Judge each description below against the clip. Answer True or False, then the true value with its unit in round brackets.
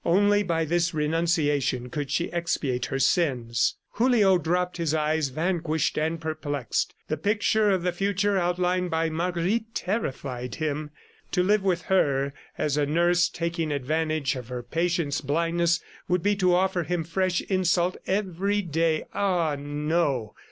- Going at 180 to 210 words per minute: False (145 wpm)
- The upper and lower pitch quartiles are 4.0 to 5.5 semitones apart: False (3.4 semitones)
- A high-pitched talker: False (170 Hz)